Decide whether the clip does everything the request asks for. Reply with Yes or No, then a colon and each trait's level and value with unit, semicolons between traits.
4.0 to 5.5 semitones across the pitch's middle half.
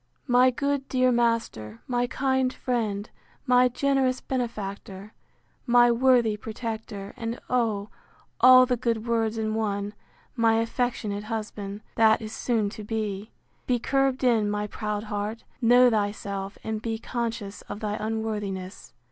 No: average, 2.9 semitones